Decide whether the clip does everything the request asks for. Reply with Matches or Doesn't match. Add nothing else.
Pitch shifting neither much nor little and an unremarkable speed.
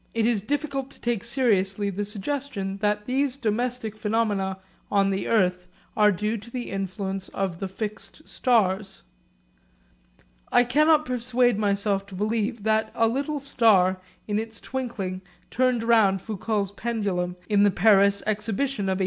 Matches